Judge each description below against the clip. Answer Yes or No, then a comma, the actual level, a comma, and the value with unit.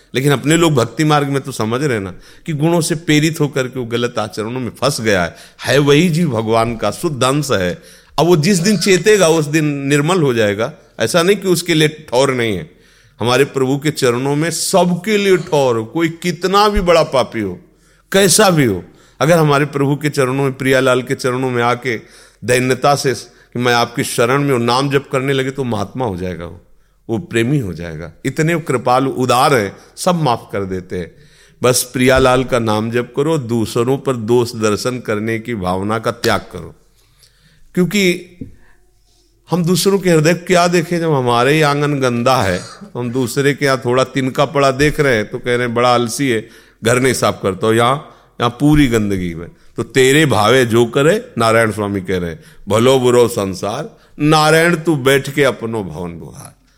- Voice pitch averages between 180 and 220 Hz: No, low, 130 Hz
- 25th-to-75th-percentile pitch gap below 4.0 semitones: No, average, 4.7 semitones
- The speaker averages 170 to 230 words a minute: Yes, fast, 190 wpm